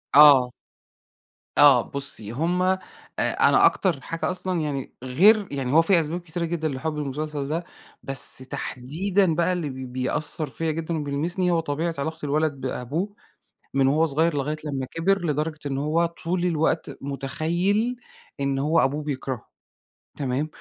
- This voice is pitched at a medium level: Yes, medium, 155 Hz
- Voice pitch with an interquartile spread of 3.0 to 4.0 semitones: Yes, average, 3.5 semitones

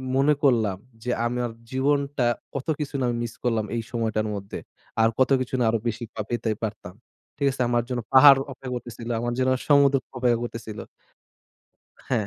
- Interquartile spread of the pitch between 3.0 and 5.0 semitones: No, narrow, 2.5 semitones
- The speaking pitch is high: No, low, 120 Hz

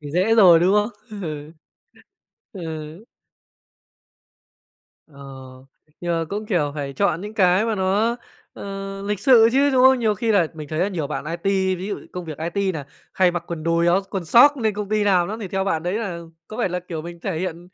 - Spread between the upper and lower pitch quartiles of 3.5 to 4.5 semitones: Yes, average, 3.8 semitones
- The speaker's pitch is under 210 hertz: Yes, medium, 185 Hz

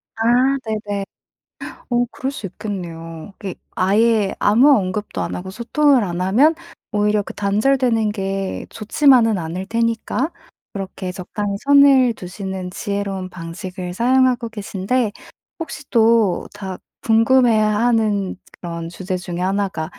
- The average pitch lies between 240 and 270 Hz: No, high, 205 Hz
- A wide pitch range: No, average, 3.8 semitones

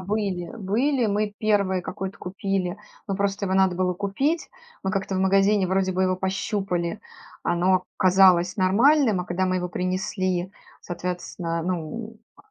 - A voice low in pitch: No, high, 190 Hz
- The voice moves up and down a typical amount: No, narrow, 1.6 semitones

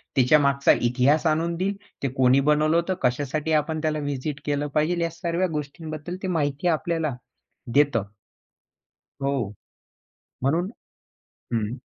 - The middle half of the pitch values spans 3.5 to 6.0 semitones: No, average, 3.0 semitones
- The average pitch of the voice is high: No, medium, 150 Hz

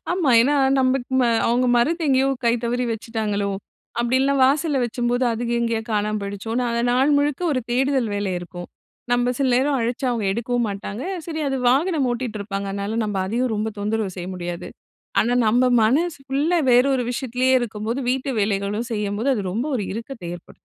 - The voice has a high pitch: Yes, high, 240 Hz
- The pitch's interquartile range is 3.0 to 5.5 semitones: Yes, average, 3.8 semitones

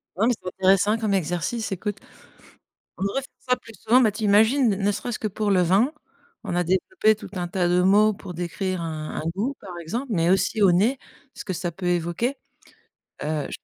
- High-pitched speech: Yes, high, 195 Hz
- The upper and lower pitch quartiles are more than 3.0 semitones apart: Yes, average, 3.7 semitones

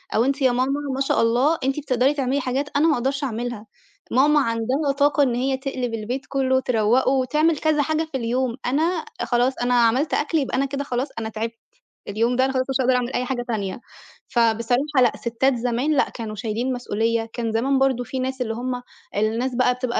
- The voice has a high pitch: Yes, very high, 255 Hz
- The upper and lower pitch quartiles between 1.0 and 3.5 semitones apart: Yes, narrow, 2.6 semitones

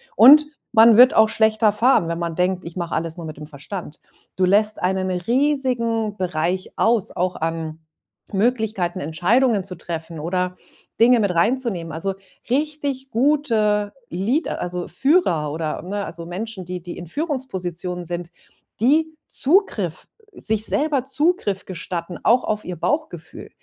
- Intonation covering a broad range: Yes, wide, 6.0 semitones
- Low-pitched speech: No, high, 195 Hz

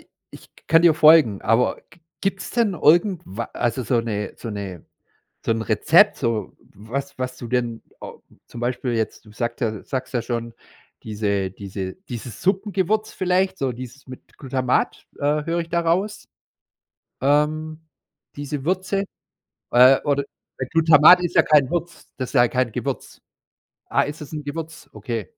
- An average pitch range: No, wide, 5.8 semitones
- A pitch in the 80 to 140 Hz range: Yes, low, 135 Hz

